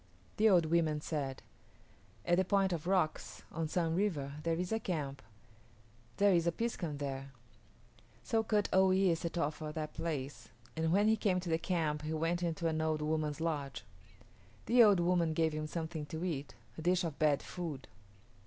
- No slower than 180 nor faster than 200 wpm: Yes, average, 185 wpm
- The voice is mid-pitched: Yes, medium, 165 Hz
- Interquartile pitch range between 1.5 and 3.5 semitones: Yes, average, 3.0 semitones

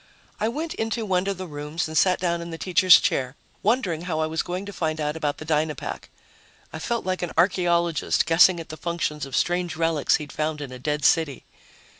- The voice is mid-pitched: Yes, medium, 165 Hz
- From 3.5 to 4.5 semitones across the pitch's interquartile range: No, average, 3.0 semitones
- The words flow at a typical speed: No, fast, 215 wpm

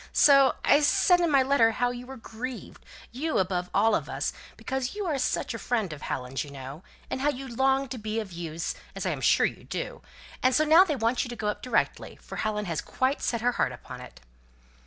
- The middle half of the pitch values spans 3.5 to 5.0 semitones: Yes, average, 4.5 semitones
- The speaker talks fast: Yes, fast, 235 wpm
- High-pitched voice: Yes, high, 245 Hz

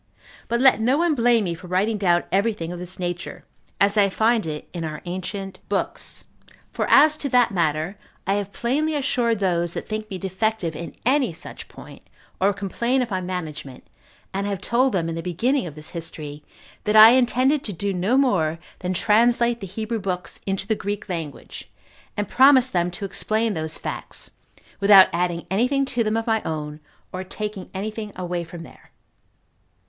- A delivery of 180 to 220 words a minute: Yes, average, 190 wpm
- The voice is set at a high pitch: Yes, high, 200 Hz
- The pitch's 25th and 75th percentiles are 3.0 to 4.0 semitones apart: No, average, 4.8 semitones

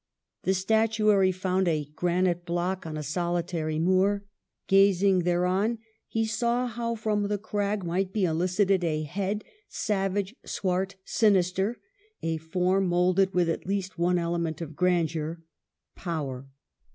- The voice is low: No, medium, 185 Hz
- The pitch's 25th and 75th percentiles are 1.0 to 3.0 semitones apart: Yes, average, 2.7 semitones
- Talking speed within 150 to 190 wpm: No, average, 140 wpm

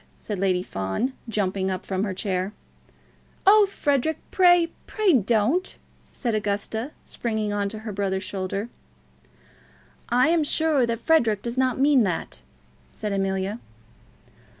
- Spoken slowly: Yes, slow, 125 wpm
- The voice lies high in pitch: Yes, high, 215 Hz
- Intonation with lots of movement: Yes, wide, 5.9 semitones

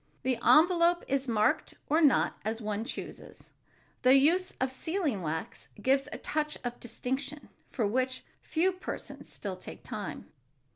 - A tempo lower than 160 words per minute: Yes, average, 150 wpm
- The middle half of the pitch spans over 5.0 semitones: Yes, wide, 5.4 semitones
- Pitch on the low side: No, very high, 260 Hz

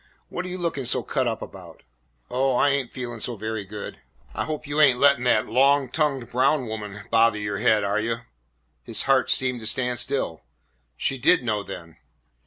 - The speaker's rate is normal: Yes, average, 195 wpm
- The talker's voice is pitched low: Yes, low, 125 Hz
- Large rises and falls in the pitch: No, average, 4.1 semitones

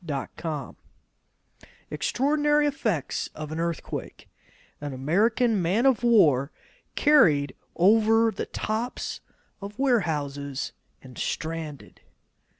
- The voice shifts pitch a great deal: Yes, wide, 8.0 semitones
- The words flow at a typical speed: No, slow, 85 wpm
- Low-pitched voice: No, high, 195 Hz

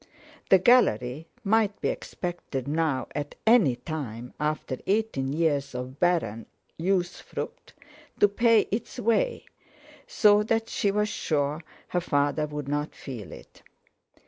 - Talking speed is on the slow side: Yes, slow, 125 wpm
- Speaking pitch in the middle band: Yes, medium, 160 Hz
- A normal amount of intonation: No, wide, 6.9 semitones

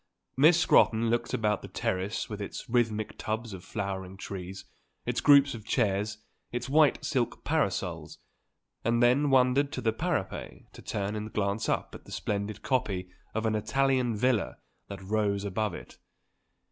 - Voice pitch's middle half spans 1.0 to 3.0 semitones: No, average, 3.9 semitones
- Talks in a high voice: No, low, 110 Hz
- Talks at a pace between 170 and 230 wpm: No, average, 160 wpm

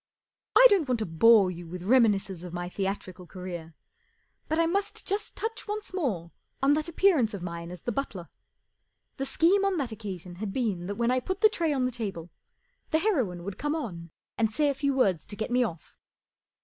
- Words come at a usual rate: No, fast, 215 wpm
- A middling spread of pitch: No, wide, 8.7 semitones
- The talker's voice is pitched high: Yes, high, 225 Hz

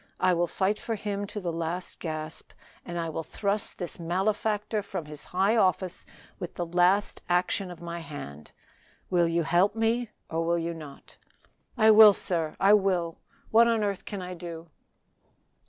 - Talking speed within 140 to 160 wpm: No, average, 170 wpm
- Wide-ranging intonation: No, average, 3.5 semitones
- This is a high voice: No, medium, 180 Hz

